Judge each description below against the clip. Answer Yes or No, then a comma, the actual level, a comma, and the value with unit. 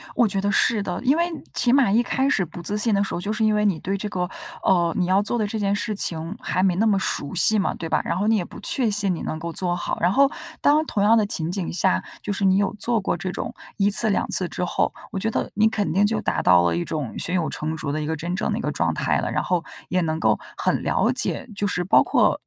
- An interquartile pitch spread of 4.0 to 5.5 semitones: No, average, 3.5 semitones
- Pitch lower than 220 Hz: Yes, high, 195 Hz